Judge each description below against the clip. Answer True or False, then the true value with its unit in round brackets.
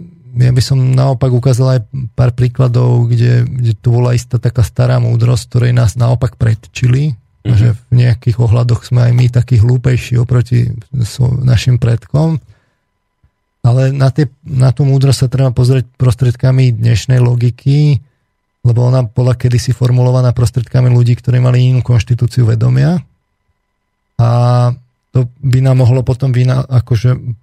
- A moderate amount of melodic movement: False (1.3 semitones)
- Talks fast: False (140 wpm)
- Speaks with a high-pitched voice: False (125 Hz)